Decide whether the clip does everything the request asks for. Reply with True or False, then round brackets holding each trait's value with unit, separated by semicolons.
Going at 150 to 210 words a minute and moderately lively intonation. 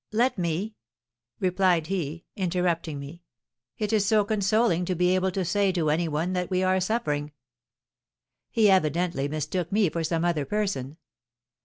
True (155 wpm; 3.2 semitones)